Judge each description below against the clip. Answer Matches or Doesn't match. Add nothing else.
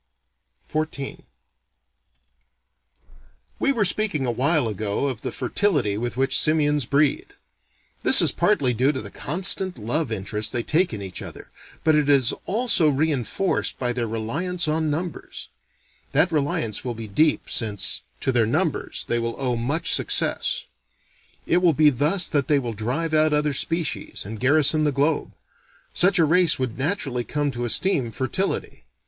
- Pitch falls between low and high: Matches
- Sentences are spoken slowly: Doesn't match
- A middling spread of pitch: Matches